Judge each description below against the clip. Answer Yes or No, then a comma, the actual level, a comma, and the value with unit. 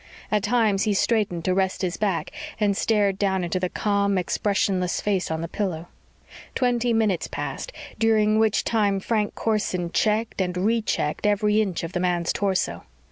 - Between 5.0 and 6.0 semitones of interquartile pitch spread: No, average, 2.8 semitones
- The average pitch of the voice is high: Yes, high, 200 Hz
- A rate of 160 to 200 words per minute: Yes, average, 165 wpm